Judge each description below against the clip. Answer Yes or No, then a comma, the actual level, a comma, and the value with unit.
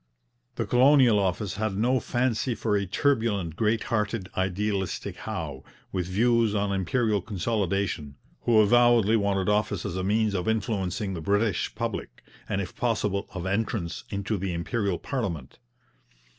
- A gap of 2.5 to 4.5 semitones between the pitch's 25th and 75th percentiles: Yes, average, 3.2 semitones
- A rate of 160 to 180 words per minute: No, average, 145 wpm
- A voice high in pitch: No, low, 100 Hz